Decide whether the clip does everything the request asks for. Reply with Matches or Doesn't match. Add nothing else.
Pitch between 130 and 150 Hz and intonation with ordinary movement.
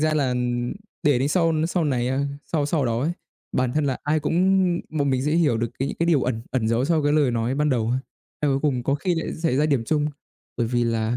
Matches